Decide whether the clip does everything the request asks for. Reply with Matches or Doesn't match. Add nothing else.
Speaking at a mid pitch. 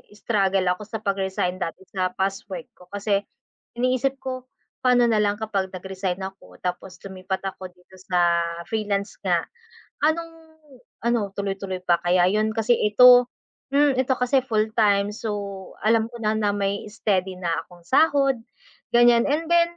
Doesn't match